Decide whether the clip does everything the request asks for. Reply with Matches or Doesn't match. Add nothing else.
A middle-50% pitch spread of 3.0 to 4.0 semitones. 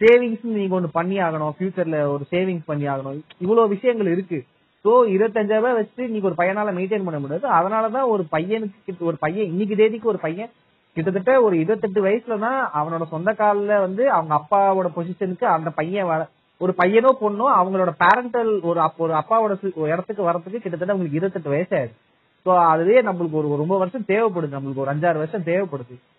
Doesn't match